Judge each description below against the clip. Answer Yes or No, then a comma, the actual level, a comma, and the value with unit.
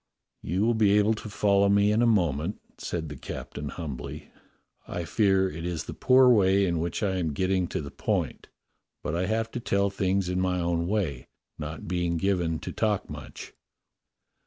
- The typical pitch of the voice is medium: No, very low, 95 Hz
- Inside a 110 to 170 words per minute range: No, average, 185 wpm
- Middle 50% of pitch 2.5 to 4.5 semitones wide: Yes, average, 3.3 semitones